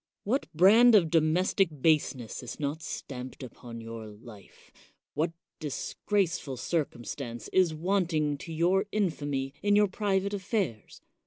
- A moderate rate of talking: No, slow, 125 wpm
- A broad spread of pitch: Yes, wide, 6.6 semitones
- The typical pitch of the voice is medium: Yes, medium, 160 Hz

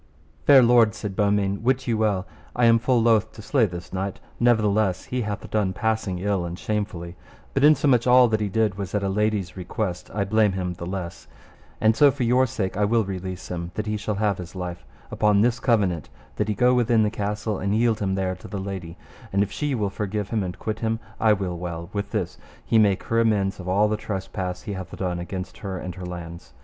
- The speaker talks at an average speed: No, fast, 225 wpm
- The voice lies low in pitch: Yes, low, 105 Hz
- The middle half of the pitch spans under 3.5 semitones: Yes, average, 3.1 semitones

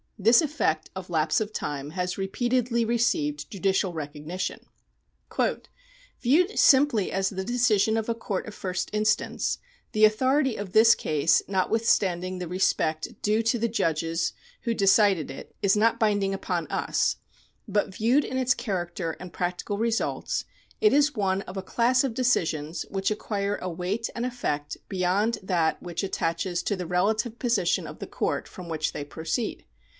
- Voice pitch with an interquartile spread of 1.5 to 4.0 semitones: No, average, 4.4 semitones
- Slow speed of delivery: No, average, 160 wpm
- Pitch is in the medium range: No, high, 200 Hz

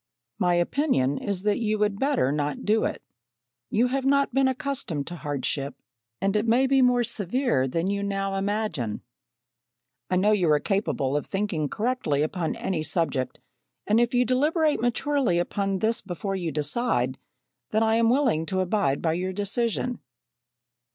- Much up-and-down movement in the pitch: Yes, wide, 6.5 semitones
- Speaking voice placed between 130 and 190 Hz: No, high, 200 Hz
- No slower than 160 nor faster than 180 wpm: Yes, average, 165 wpm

